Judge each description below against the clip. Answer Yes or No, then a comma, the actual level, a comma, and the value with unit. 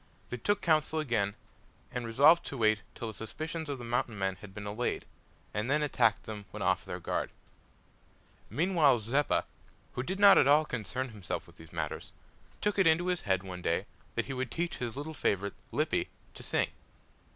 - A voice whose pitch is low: Yes, low, 125 Hz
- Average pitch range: No, wide, 6.7 semitones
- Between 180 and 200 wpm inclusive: Yes, average, 190 wpm